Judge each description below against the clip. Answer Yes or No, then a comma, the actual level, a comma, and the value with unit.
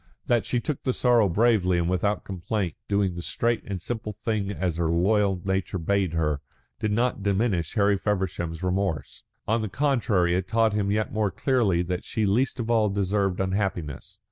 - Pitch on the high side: No, low, 100 Hz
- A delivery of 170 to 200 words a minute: Yes, average, 180 wpm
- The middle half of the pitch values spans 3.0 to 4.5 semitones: Yes, average, 3.3 semitones